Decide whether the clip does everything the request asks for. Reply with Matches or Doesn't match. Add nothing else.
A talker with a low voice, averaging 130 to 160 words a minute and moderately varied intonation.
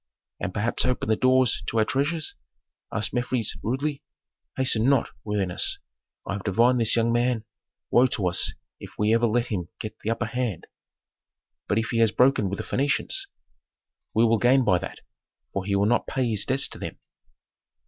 Doesn't match